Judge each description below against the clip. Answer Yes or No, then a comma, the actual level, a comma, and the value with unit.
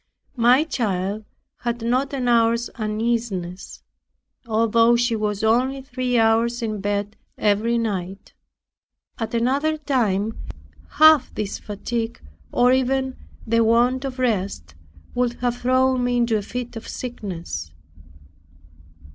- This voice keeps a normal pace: No, slow, 120 wpm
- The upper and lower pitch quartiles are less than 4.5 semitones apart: Yes, average, 2.8 semitones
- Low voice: No, high, 235 Hz